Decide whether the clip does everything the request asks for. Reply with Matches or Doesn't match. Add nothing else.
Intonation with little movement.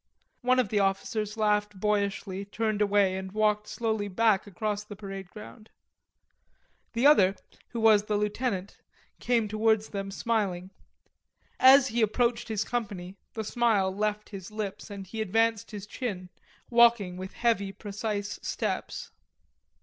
Matches